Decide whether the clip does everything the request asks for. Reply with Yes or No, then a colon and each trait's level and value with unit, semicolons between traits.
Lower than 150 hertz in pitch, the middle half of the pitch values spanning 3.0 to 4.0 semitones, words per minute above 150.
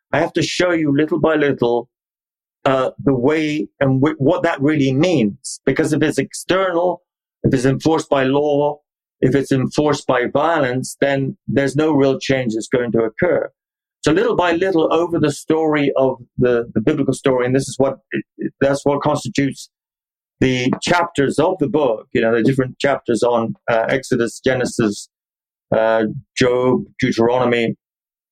Yes: low, 135 Hz; average, 3.4 semitones; average, 165 wpm